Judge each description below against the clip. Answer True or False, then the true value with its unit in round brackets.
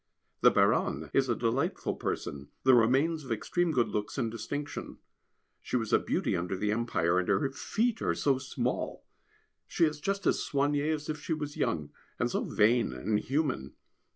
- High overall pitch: False (130 Hz)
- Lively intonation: True (6.0 semitones)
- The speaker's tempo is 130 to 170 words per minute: False (180 wpm)